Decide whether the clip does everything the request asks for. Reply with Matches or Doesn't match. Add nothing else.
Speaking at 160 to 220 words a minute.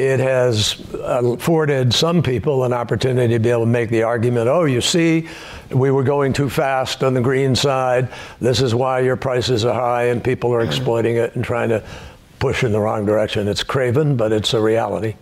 Matches